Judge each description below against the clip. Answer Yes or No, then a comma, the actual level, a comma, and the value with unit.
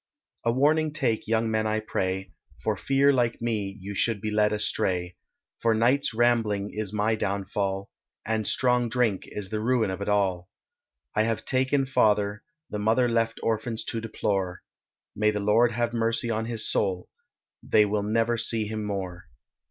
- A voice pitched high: No, low, 110 Hz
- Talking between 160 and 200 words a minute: Yes, average, 165 wpm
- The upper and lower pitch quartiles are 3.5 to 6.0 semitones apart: No, narrow, 2.4 semitones